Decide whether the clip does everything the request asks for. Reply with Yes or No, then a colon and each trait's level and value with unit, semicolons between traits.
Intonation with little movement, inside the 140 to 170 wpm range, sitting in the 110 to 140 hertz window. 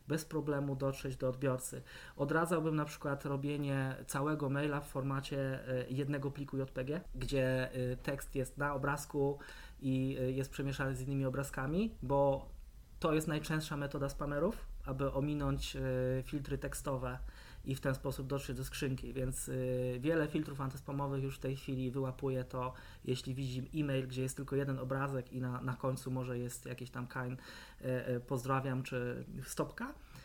Yes: narrow, 1.6 semitones; average, 155 wpm; low, 135 Hz